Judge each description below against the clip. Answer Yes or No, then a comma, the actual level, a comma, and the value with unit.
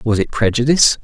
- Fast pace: No, average, 175 wpm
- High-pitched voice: No, low, 120 Hz